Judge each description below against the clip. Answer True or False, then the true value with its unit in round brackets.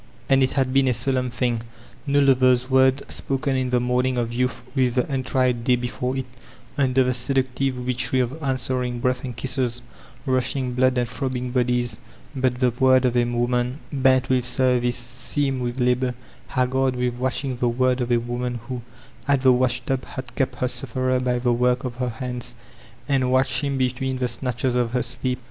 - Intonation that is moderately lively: False (1.1 semitones)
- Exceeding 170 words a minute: True (195 wpm)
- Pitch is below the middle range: True (125 Hz)